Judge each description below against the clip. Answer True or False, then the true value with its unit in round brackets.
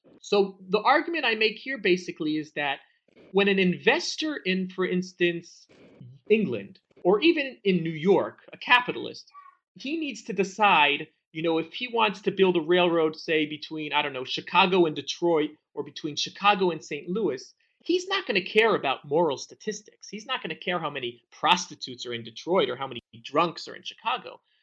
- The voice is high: False (180 Hz)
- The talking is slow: False (185 wpm)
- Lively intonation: True (5.9 semitones)